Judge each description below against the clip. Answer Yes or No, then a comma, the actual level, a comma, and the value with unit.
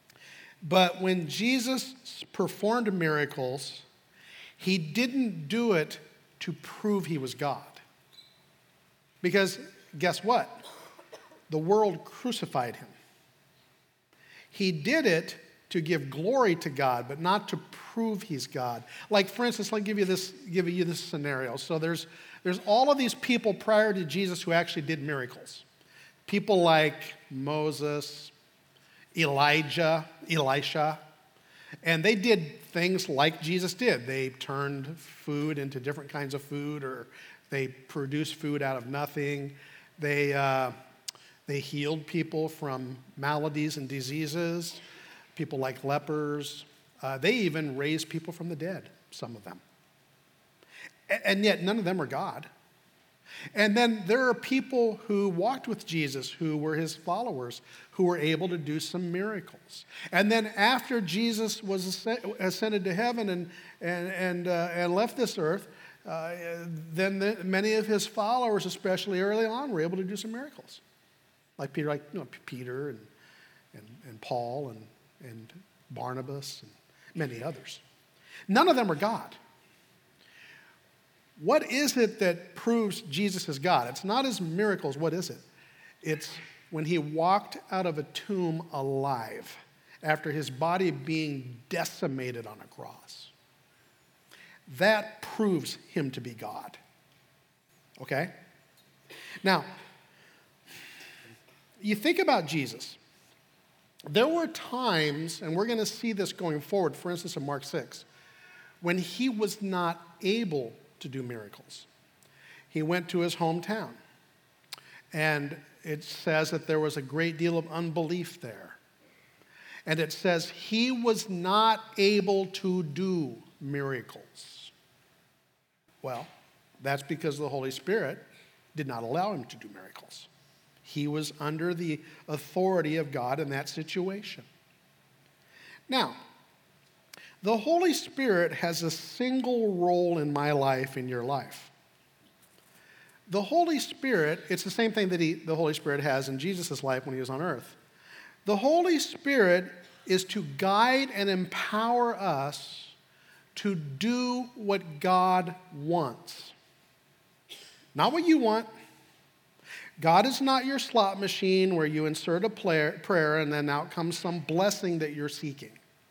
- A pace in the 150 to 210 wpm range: No, average, 140 wpm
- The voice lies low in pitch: No, medium, 170 Hz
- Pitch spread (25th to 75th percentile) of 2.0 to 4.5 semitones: No, average, 5.2 semitones